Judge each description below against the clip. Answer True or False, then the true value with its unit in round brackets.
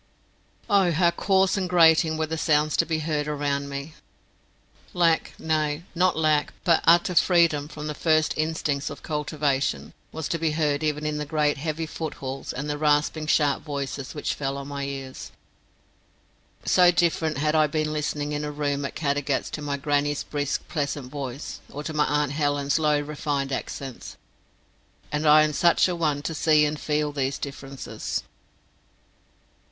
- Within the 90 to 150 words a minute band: False (170 wpm)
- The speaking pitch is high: False (150 Hz)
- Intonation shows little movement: True (1.7 semitones)